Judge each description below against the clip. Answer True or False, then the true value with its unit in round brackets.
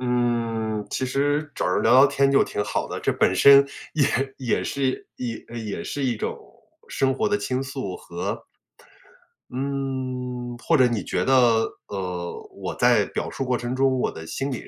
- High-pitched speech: False (130 Hz)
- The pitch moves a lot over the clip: False (2.9 semitones)